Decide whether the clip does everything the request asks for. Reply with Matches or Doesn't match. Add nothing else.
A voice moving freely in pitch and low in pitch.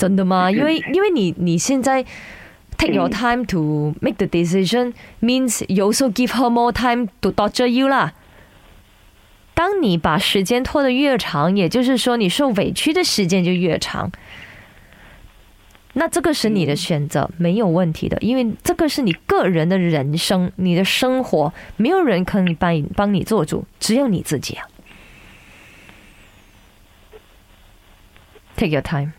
Doesn't match